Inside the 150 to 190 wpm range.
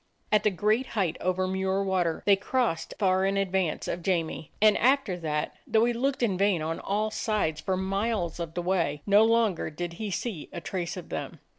No: average, 200 wpm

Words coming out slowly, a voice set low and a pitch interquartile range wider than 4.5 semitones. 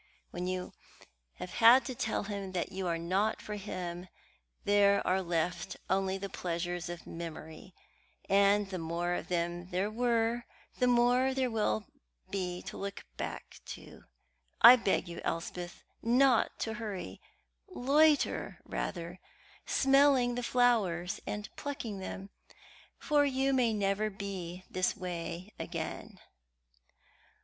No: slow, 130 wpm; high, 195 Hz; average, 4.9 semitones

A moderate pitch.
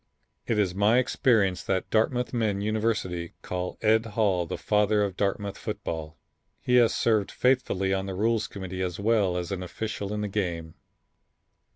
No: low, 100 Hz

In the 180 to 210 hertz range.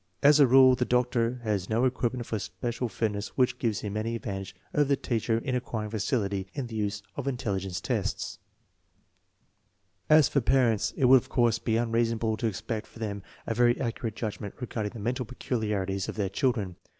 No: low, 115 Hz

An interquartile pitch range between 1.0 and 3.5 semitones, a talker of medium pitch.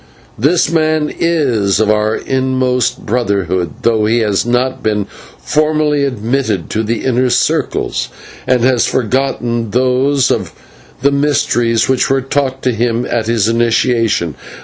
No: average, 3.2 semitones; low, 125 Hz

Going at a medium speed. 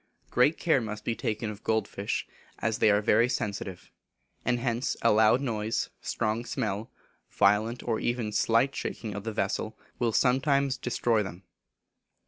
Yes: average, 155 wpm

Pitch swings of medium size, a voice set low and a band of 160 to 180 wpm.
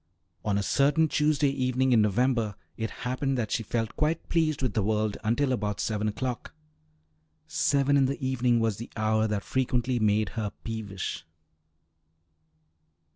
No: average, 3.8 semitones; low, 120 Hz; average, 150 wpm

